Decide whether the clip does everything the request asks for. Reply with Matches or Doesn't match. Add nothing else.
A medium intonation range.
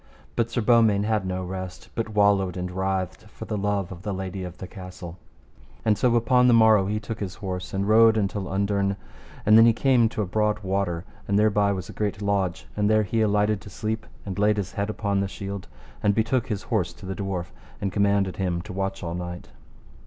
Doesn't match